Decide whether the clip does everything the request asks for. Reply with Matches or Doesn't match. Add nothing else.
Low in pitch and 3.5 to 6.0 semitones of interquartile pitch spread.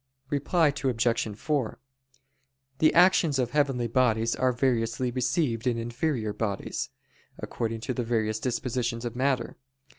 Doesn't match